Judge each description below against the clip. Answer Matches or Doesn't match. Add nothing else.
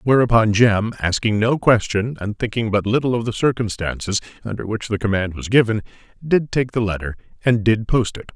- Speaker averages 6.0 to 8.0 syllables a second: Doesn't match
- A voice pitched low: Matches